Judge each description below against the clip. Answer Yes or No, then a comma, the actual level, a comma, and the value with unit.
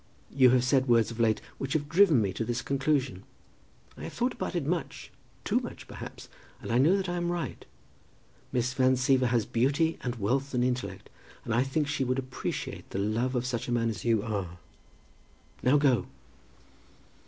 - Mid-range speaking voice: No, low, 130 Hz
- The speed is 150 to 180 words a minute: No, average, 195 wpm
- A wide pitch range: No, average, 3.3 semitones